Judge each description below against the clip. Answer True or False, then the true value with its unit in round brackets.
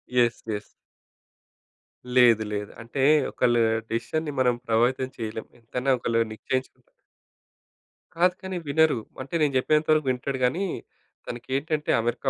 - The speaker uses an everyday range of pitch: True (4.1 semitones)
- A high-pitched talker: False (130 Hz)